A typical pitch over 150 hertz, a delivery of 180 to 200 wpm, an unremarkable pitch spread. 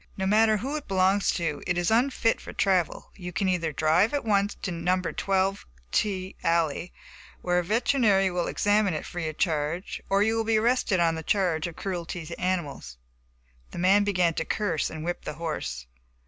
Yes: medium, 185 Hz; average, 190 wpm; average, 3.5 semitones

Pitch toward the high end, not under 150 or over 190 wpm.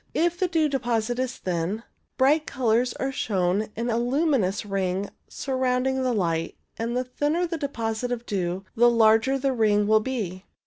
Yes: high, 235 Hz; average, 170 wpm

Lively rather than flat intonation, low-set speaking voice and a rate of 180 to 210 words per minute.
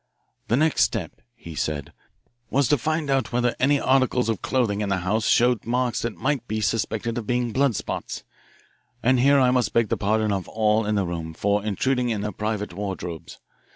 No: average, 3.7 semitones; low, 115 Hz; average, 195 wpm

